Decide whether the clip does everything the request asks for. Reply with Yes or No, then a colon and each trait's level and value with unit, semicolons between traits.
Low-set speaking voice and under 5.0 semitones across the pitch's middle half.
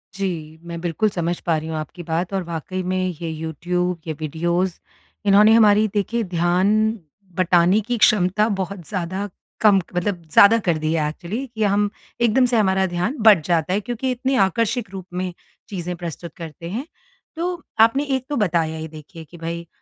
No: medium, 180 Hz; average, 3.8 semitones